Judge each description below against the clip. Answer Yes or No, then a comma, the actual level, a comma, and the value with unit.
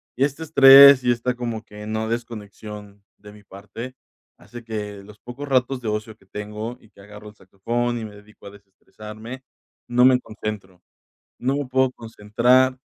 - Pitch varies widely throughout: No, average, 3.2 semitones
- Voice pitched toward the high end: No, low, 110 Hz